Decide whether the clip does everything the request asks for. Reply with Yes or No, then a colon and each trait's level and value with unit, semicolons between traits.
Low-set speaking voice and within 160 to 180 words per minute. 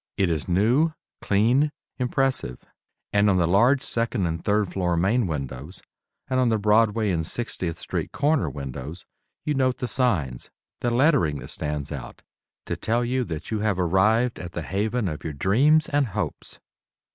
Yes: low, 105 Hz; average, 170 wpm